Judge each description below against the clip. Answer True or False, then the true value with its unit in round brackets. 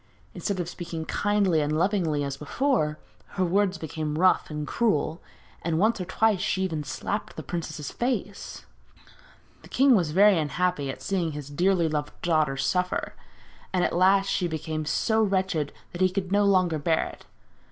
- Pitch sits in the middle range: True (175 Hz)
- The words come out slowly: False (170 wpm)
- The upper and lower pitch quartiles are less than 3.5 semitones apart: False (4.1 semitones)